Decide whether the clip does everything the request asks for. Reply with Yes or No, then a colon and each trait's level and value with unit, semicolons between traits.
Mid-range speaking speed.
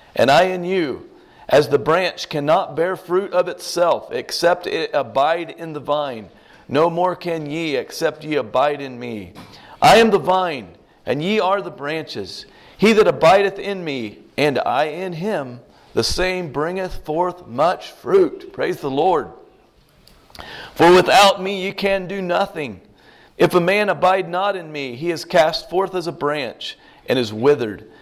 Yes: average, 165 wpm